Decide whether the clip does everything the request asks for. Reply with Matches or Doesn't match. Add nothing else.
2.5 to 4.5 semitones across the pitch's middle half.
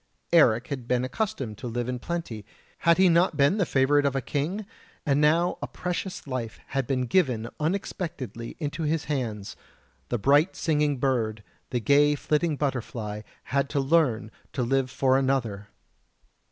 Matches